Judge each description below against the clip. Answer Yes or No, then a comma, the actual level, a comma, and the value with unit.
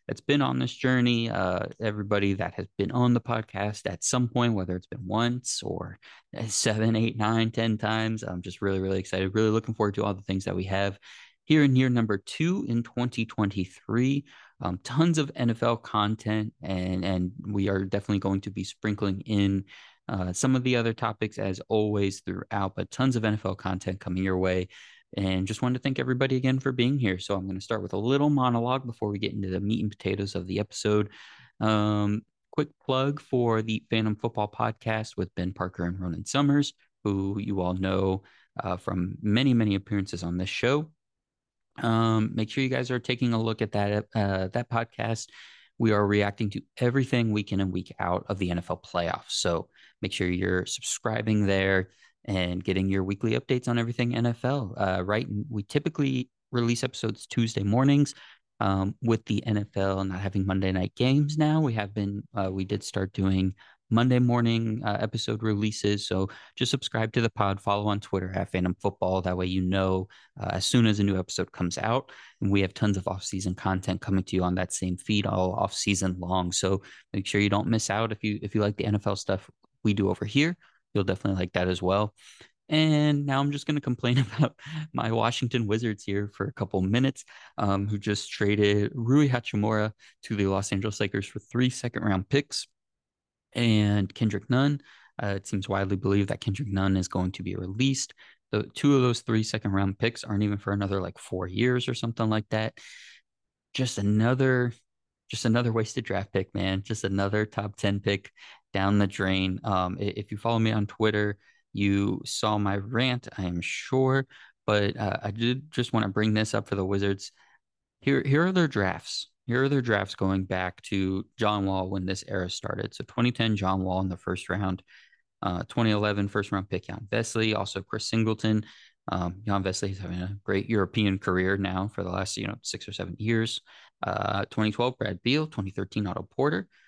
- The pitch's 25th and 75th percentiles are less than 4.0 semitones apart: Yes, average, 3.4 semitones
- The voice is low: Yes, low, 105 Hz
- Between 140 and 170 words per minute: No, average, 195 wpm